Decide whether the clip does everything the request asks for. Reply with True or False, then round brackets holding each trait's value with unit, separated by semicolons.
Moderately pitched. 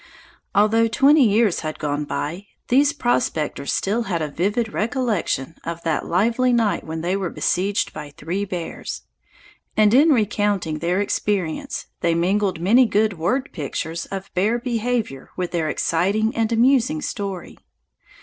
False (200 Hz)